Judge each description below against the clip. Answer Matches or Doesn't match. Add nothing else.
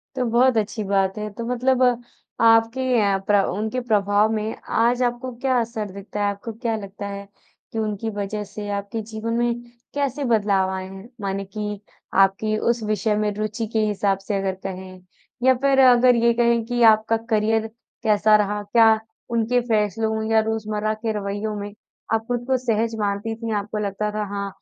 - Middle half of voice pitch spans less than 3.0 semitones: Matches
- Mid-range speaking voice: Doesn't match